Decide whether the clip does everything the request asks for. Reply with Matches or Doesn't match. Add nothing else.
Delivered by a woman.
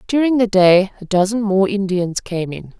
Matches